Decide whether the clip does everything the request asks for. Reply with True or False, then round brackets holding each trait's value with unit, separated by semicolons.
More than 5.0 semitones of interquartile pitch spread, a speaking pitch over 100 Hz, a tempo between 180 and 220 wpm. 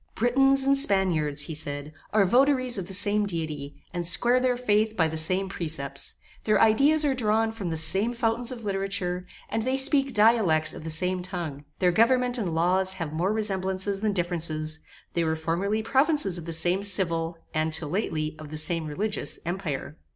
True (5.6 semitones; 190 Hz; 185 wpm)